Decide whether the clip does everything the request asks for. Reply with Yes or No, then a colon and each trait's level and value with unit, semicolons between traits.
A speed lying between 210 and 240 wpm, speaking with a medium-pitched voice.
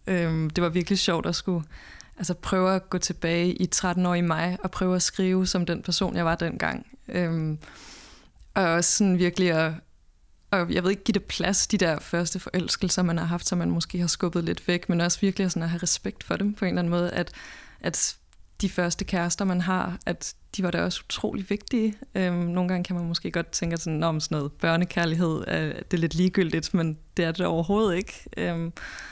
Yes: average, 220 wpm; medium, 180 Hz